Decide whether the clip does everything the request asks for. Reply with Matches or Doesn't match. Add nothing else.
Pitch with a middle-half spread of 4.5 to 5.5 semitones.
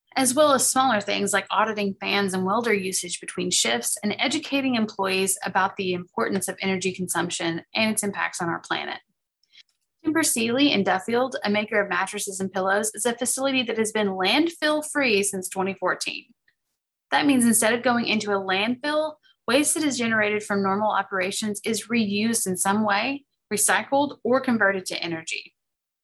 Matches